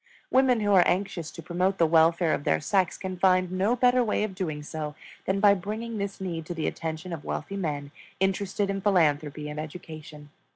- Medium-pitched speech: Yes, medium, 180 Hz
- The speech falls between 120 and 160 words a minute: No, average, 200 wpm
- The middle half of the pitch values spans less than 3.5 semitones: No, average, 4.0 semitones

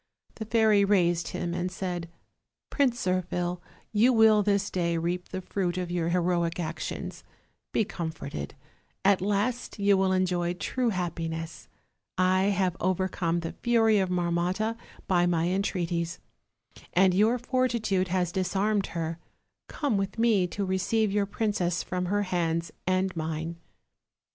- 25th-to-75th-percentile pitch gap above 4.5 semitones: No, average, 2.8 semitones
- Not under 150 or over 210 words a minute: No, average, 140 wpm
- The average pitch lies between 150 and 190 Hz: Yes, medium, 185 Hz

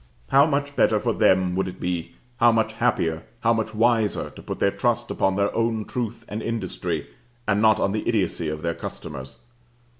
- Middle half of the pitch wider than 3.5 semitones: Yes, average, 4.3 semitones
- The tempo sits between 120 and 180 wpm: No, average, 190 wpm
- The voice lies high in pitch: No, low, 105 Hz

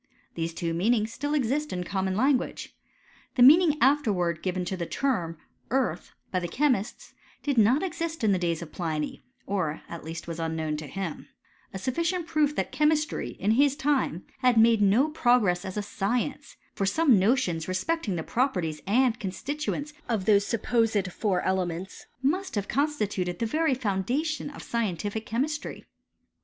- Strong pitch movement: Yes, wide, 7.5 semitones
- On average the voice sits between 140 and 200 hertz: No, high, 220 Hz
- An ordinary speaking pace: Yes, average, 160 wpm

